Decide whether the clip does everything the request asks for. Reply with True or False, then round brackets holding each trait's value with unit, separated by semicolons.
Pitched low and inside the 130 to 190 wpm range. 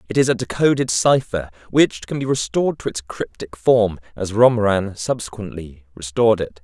True (110 Hz; 165 wpm)